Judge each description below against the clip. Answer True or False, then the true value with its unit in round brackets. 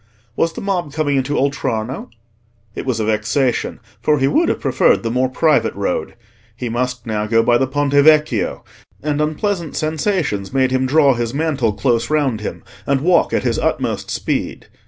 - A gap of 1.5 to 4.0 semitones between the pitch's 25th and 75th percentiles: False (4.5 semitones)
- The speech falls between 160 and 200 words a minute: True (175 wpm)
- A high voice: False (135 Hz)